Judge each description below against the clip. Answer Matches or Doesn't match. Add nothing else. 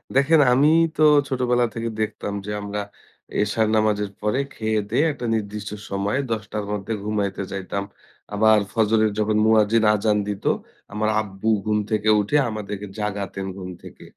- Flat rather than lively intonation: Matches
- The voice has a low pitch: Matches